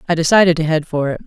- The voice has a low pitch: No, medium, 160 Hz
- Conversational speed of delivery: No, fast, 285 wpm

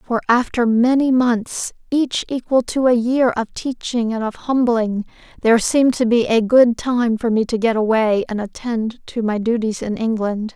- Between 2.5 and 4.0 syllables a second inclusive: No, 4.5 syllables/s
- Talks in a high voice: Yes, high, 235 Hz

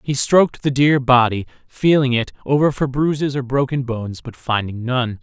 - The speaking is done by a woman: No, male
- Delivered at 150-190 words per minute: Yes, average, 185 wpm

